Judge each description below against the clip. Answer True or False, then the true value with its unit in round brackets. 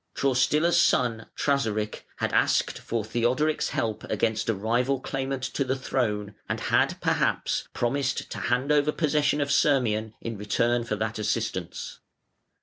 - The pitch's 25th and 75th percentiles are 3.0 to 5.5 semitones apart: True (3.9 semitones)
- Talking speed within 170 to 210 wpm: False (145 wpm)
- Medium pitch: False (120 Hz)